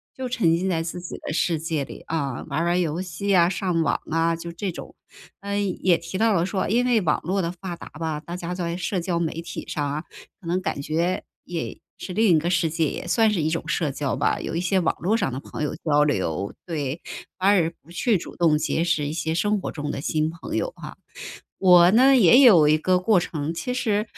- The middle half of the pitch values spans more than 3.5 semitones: No, average, 2.9 semitones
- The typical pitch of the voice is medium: Yes, medium, 170 Hz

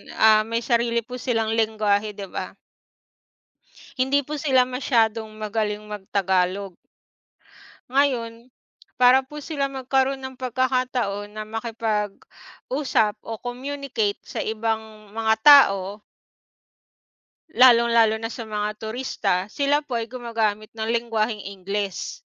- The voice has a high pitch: Yes, high, 230 Hz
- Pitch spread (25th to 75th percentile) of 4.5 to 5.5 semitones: No, average, 3.2 semitones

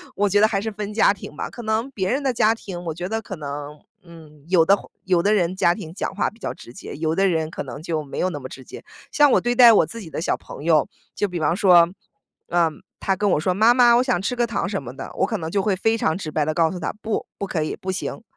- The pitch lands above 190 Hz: No, medium, 185 Hz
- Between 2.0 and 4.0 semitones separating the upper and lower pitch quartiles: No, average, 5.1 semitones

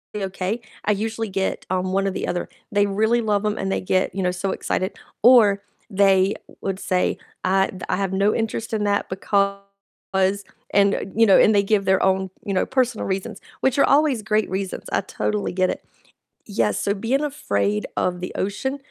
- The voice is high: Yes, high, 200 Hz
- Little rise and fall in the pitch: Yes, narrow, 2.0 semitones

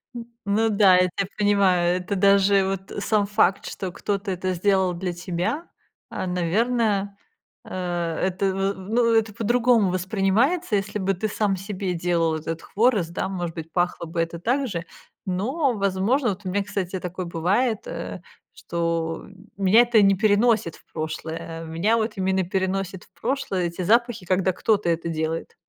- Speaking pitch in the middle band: No, high, 195 Hz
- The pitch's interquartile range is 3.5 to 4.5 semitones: No, average, 3.1 semitones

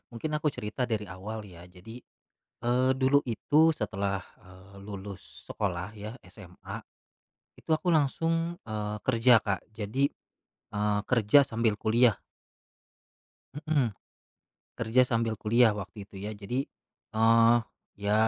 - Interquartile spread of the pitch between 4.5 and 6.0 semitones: No, average, 3.8 semitones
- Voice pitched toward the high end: No, low, 110 Hz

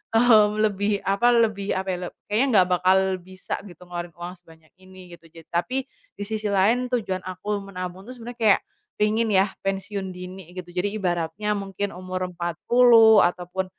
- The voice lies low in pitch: No, high, 190 Hz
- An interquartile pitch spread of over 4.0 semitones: No, average, 2.8 semitones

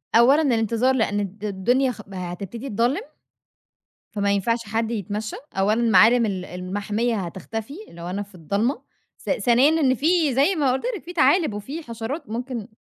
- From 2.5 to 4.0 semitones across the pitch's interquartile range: No, average, 4.4 semitones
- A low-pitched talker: No, high, 225 Hz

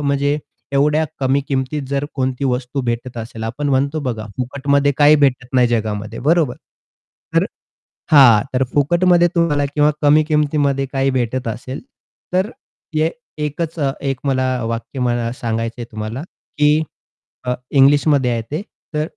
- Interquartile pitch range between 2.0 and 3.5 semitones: Yes, average, 3.1 semitones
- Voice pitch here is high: No, low, 135 Hz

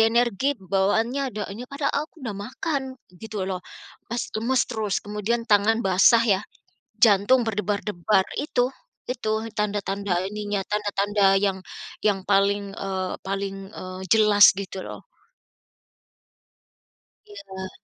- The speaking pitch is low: No, high, 205 Hz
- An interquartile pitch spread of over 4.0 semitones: No, average, 2.9 semitones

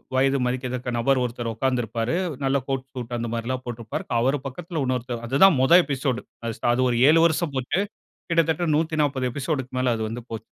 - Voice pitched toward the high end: No, low, 130 Hz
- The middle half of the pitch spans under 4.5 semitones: Yes, average, 2.8 semitones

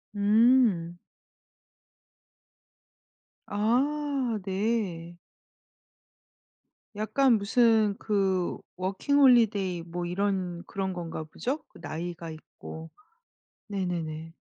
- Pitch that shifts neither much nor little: Yes, average, 4.7 semitones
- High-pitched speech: Yes, high, 195 Hz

